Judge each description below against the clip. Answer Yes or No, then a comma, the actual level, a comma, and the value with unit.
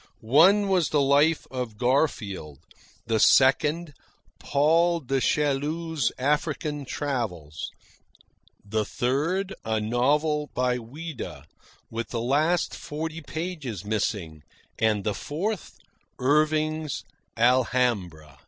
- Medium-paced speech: No, slow, 95 wpm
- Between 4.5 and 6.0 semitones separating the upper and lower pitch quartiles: Yes, wide, 5.4 semitones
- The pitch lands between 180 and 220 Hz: No, medium, 140 Hz